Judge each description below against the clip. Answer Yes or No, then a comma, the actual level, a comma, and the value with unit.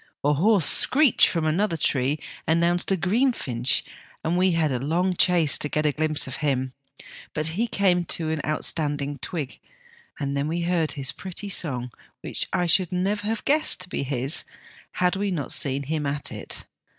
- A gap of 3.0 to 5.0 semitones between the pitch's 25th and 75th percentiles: Yes, average, 4.2 semitones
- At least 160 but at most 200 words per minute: Yes, average, 185 wpm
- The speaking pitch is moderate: Yes, medium, 160 Hz